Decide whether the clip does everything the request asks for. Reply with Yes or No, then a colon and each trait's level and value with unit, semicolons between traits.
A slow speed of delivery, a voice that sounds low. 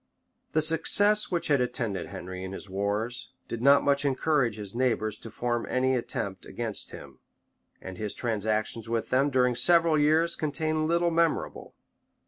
No: average, 155 wpm; low, 125 Hz